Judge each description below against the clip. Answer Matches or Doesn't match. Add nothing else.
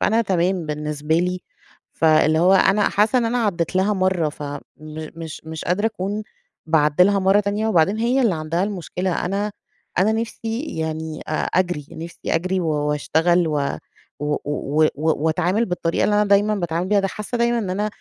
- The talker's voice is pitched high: Doesn't match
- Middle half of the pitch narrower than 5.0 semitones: Matches